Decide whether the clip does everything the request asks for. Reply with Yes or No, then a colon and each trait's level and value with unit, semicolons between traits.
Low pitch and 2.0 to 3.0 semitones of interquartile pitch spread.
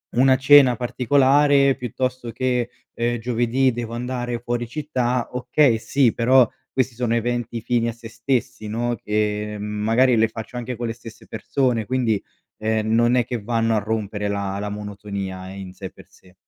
Yes: low, 120 Hz; narrow, 2.6 semitones